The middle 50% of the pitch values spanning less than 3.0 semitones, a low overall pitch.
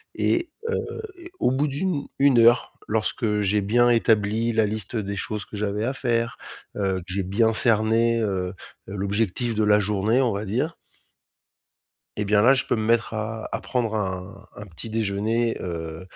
Yes: narrow, 2.6 semitones; low, 110 Hz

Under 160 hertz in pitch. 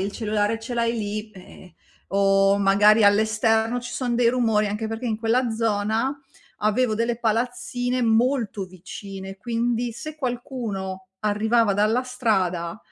No: high, 220 Hz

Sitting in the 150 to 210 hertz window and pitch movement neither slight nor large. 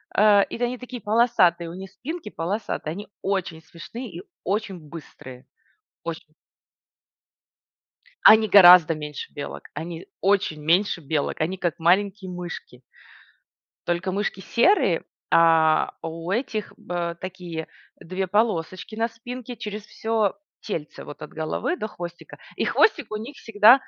Yes: high, 190 Hz; average, 4.6 semitones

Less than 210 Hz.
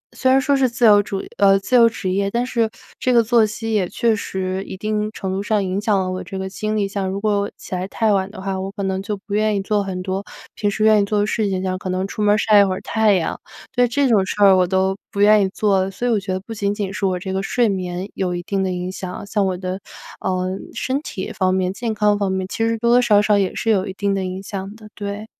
Yes: high, 200 Hz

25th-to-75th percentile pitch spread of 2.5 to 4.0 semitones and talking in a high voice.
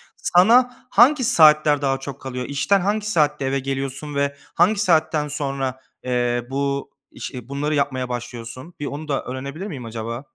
No: average, 3.2 semitones; medium, 140 Hz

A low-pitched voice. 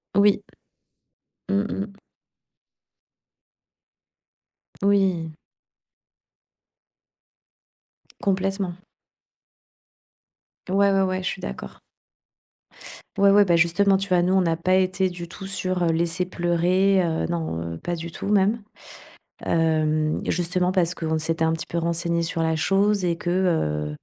No: medium, 175 Hz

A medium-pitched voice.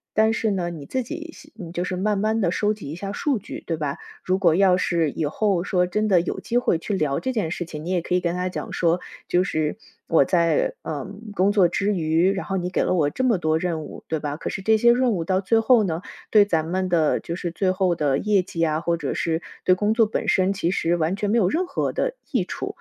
Yes: medium, 180 Hz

